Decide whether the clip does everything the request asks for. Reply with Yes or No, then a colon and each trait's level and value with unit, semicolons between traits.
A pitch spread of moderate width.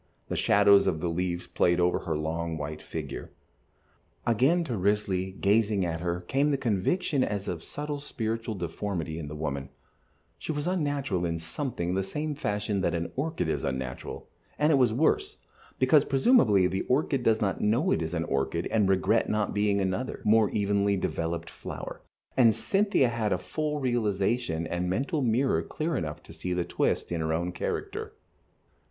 No: wide, 7.0 semitones